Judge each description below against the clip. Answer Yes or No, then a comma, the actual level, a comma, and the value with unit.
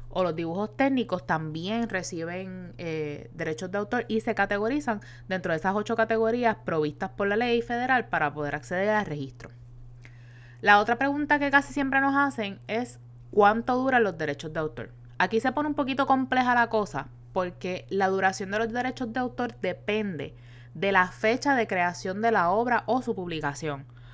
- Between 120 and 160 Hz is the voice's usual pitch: No, high, 195 Hz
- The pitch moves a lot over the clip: Yes, wide, 7.0 semitones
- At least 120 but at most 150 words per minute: No, average, 175 wpm